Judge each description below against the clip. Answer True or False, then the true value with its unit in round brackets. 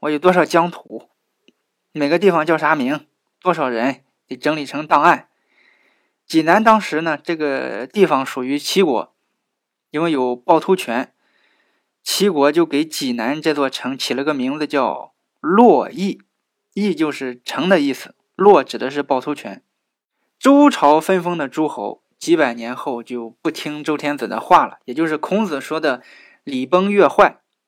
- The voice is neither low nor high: True (155 Hz)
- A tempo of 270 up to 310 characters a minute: False (230 characters per minute)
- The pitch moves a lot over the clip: False (5.0 semitones)